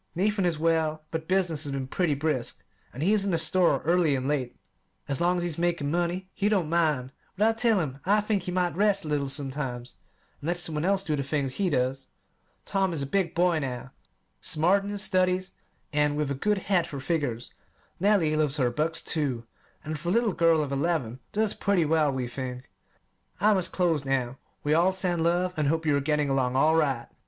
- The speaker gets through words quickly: Yes, fast, 220 wpm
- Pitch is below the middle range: No, medium, 160 Hz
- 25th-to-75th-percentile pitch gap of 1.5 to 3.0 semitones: No, average, 4.6 semitones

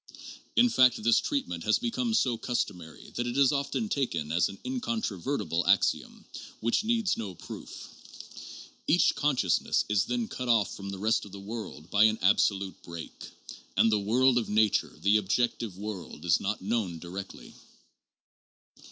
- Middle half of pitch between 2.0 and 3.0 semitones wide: No, average, 4.9 semitones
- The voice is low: Yes, low, 110 Hz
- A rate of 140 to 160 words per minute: Yes, average, 155 wpm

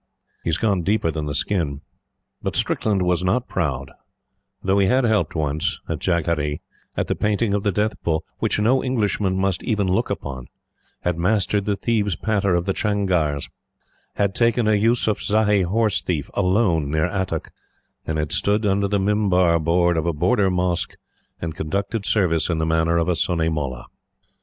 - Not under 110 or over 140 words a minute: No, average, 175 wpm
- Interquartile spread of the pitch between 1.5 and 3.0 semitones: No, average, 4.1 semitones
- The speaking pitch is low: Yes, very low, 95 Hz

